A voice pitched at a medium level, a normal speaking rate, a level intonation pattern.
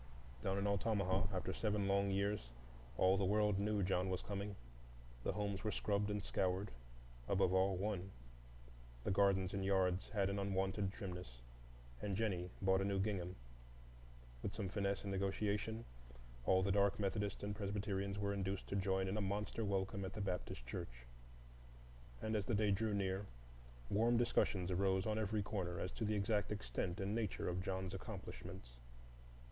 No: low, 100 Hz; average, 165 wpm; narrow, 1.6 semitones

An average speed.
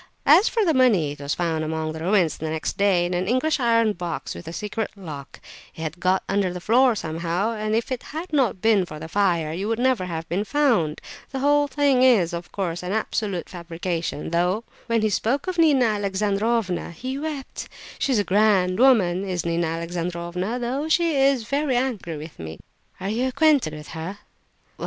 Yes: average, 195 wpm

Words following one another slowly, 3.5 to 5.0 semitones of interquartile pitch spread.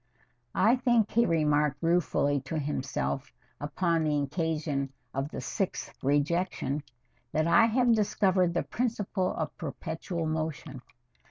Yes: slow, 120 wpm; average, 4.4 semitones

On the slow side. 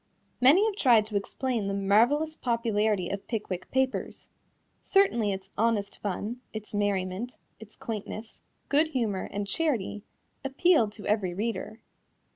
Yes: slow, 130 wpm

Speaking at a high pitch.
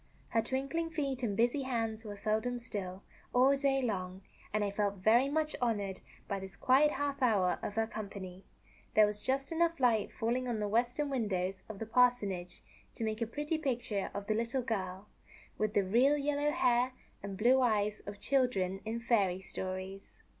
Yes: high, 225 Hz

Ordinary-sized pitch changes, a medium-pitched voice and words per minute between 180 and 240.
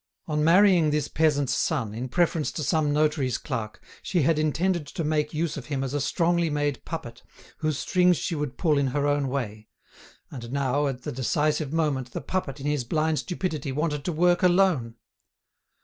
Yes: average, 3.3 semitones; medium, 150 Hz; average, 185 wpm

